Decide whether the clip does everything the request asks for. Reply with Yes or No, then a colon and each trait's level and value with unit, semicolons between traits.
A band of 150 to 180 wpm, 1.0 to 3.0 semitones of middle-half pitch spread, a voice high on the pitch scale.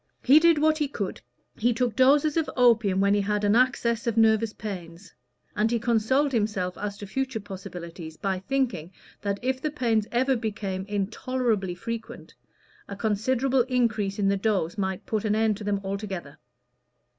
No: average, 170 wpm; average, 4.0 semitones; high, 215 Hz